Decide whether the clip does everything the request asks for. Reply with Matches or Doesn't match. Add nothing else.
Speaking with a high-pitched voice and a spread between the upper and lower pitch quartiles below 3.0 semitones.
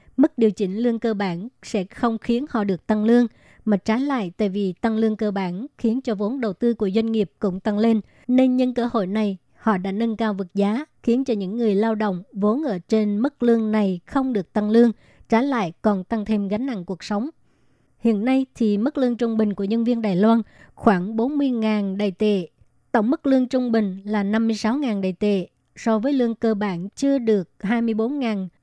Matches